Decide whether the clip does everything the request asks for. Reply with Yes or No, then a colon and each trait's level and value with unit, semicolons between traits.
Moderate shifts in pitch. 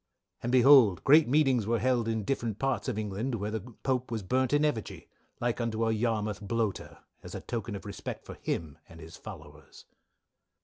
Yes: average, 3.5 semitones